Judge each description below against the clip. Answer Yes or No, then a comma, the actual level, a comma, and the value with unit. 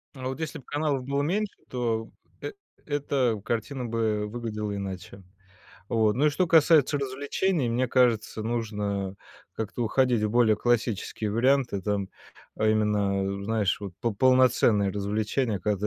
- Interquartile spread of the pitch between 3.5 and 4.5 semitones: Yes, average, 3.9 semitones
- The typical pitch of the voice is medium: No, low, 115 Hz